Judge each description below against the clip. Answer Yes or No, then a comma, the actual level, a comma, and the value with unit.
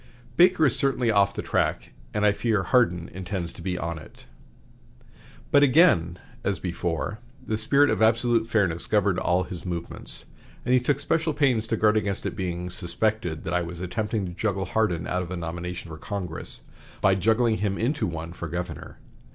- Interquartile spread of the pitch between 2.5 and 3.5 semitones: No, average, 4.5 semitones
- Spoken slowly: No, average, 185 wpm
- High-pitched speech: No, low, 100 Hz